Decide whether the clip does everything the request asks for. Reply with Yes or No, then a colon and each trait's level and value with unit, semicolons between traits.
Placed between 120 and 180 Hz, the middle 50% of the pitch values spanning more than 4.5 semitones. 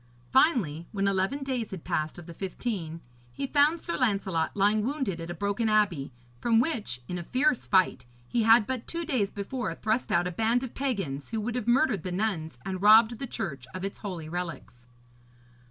No: high, 205 Hz; wide, 5.6 semitones